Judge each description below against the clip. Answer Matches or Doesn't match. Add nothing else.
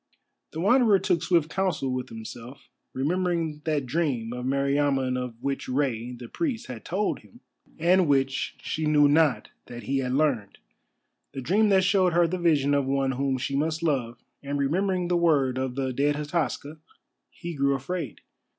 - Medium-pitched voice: Matches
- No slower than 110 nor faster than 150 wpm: Doesn't match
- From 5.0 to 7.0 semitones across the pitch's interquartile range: Doesn't match